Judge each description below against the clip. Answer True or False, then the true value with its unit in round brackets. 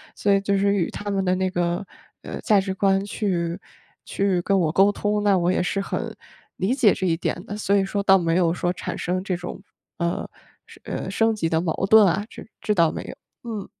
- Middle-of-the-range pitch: False (195 Hz)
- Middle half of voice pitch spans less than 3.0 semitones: True (2.4 semitones)